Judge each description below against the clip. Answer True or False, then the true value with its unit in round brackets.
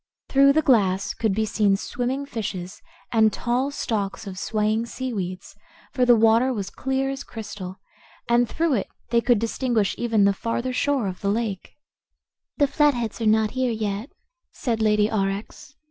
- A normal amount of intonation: True (3.8 semitones)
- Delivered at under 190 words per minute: True (160 wpm)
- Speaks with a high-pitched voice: True (225 Hz)